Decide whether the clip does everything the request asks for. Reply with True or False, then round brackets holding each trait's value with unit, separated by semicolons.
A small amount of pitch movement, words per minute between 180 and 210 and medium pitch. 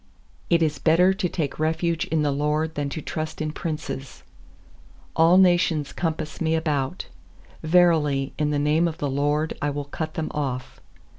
False (2.0 semitones; 165 wpm; 155 Hz)